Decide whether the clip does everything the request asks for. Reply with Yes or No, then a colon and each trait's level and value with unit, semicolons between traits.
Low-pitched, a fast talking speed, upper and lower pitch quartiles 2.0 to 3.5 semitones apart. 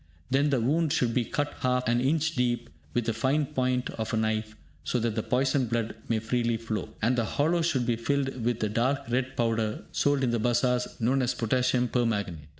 Yes: low, 125 Hz; fast, 215 wpm; narrow, 2.6 semitones